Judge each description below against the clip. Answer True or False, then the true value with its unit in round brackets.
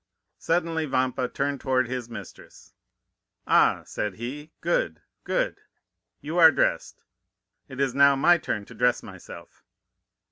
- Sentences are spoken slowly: True (120 wpm)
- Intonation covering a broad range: False (4.2 semitones)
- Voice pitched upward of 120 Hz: True (135 Hz)